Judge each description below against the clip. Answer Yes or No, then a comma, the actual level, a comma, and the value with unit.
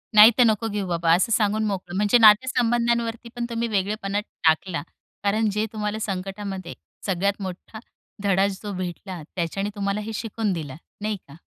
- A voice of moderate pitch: No, high, 205 Hz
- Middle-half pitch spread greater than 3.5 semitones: No, narrow, 2.6 semitones